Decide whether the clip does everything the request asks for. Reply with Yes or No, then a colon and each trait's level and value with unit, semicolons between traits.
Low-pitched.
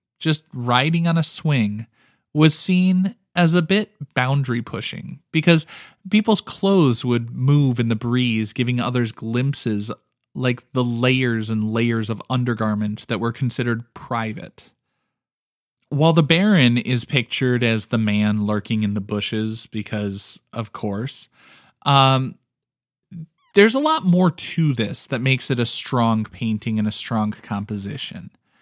Yes: low, 125 Hz